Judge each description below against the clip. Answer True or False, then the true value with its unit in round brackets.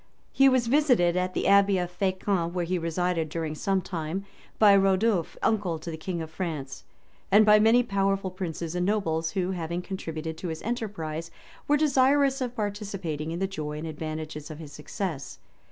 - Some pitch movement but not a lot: True (4.1 semitones)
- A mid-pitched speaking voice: True (180 Hz)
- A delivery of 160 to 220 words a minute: True (180 wpm)